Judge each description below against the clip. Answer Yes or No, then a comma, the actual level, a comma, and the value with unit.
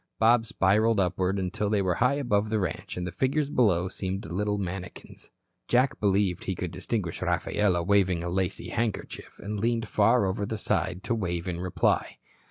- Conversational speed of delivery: Yes, average, 175 wpm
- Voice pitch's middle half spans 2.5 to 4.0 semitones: Yes, average, 3.3 semitones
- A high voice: No, low, 100 Hz